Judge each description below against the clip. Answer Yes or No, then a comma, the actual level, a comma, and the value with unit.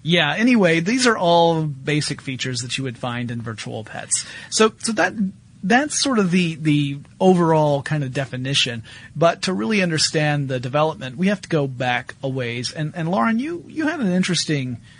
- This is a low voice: No, medium, 155 Hz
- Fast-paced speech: No, average, 190 wpm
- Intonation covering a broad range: Yes, wide, 5.9 semitones